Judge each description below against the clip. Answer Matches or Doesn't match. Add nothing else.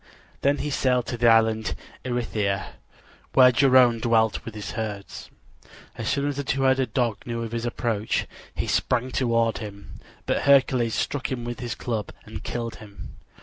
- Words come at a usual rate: Matches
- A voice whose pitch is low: Matches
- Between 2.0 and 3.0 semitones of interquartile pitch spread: Matches